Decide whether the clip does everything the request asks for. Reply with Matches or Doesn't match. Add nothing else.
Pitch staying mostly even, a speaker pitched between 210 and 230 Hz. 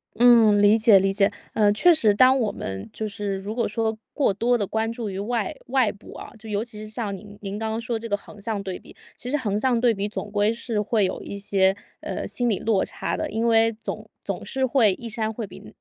Matches